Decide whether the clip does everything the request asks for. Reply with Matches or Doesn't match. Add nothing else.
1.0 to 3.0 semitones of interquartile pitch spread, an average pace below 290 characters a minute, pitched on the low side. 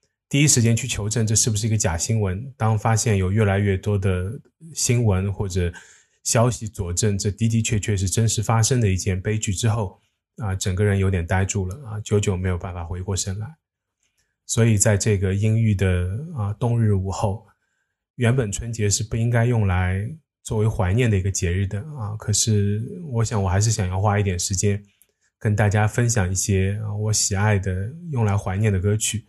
Matches